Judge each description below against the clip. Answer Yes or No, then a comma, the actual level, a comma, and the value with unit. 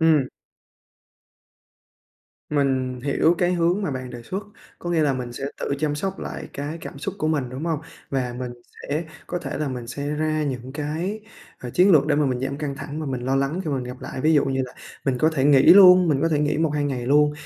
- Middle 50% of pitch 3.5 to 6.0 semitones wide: No, average, 3.1 semitones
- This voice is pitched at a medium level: Yes, medium, 145 Hz